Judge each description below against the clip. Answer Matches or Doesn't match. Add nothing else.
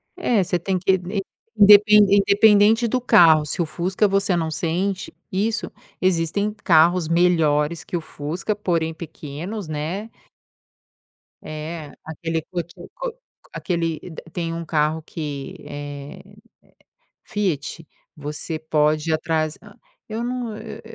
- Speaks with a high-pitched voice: Doesn't match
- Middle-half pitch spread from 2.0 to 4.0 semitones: Doesn't match